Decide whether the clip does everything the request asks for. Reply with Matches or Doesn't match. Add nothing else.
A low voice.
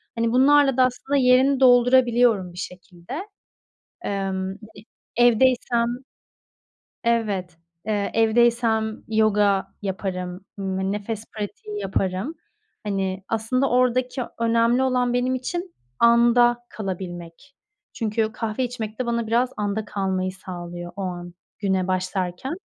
Doesn't match